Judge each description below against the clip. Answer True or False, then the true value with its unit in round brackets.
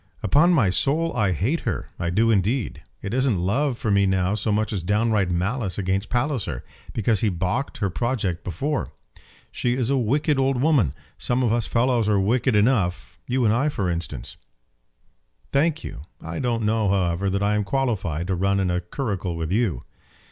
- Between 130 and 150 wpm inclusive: False (190 wpm)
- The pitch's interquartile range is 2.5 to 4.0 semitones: False (5.1 semitones)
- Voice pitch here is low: True (105 Hz)